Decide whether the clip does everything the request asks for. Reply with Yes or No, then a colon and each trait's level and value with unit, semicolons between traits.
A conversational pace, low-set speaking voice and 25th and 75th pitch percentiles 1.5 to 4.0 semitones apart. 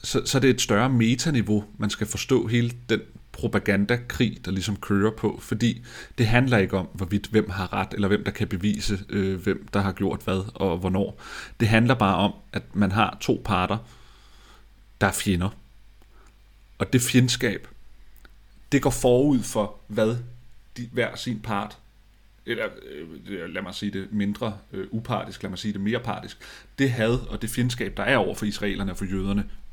Yes: average, 185 wpm; low, 105 Hz; average, 2.9 semitones